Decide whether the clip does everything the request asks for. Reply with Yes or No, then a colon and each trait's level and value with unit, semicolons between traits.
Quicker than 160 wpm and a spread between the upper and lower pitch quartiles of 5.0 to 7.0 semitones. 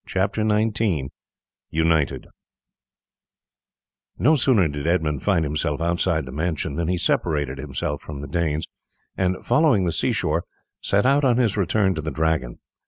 No: average, 150 wpm; wide, 5.4 semitones